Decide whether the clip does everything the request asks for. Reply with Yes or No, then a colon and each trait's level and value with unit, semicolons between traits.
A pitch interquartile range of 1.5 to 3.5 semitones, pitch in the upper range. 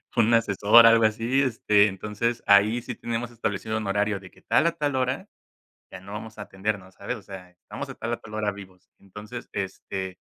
No: average, 2.9 semitones; low, 105 Hz